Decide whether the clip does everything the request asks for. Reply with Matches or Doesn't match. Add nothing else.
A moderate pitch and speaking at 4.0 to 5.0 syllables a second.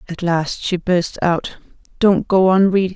Matches